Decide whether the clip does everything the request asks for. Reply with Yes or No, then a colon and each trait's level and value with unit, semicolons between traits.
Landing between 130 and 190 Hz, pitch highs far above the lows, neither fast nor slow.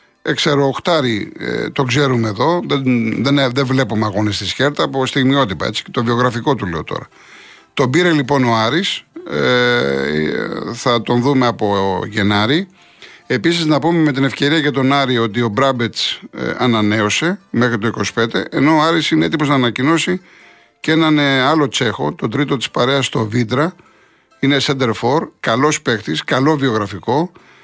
No: low, 135 Hz; average, 4.4 semitones; average, 160 wpm